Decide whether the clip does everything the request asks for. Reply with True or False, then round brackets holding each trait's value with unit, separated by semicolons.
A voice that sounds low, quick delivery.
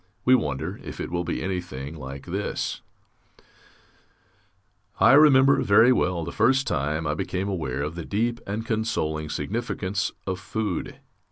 False (95 Hz; 145 wpm)